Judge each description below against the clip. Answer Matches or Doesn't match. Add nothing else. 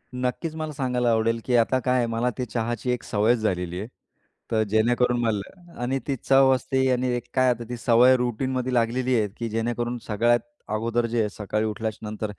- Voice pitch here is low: Matches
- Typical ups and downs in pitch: Doesn't match